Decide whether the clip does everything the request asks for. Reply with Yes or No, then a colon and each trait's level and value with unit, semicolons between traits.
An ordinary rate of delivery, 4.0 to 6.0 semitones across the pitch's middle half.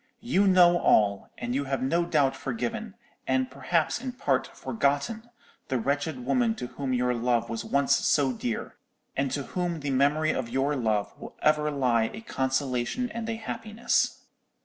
Yes: average, 170 wpm; wide, 5.6 semitones